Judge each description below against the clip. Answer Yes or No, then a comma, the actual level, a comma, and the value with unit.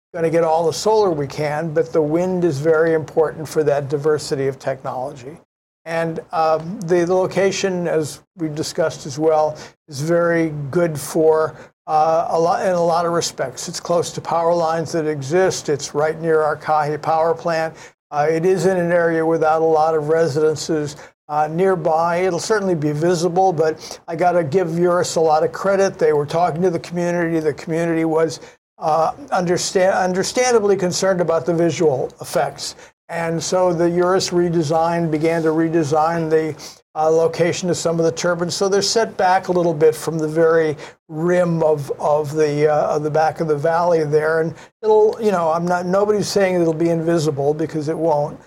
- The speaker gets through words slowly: No, average, 185 wpm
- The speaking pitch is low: No, medium, 165 Hz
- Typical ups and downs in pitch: No, narrow, 2.1 semitones